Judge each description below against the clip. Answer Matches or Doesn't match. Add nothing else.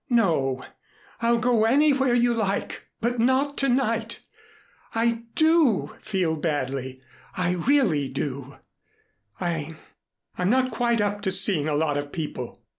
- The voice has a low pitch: Doesn't match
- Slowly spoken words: Matches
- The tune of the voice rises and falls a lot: Matches